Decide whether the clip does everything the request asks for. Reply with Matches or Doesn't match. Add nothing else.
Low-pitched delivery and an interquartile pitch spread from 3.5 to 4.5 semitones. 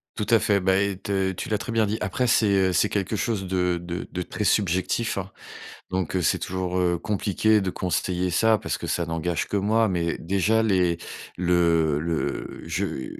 Doesn't match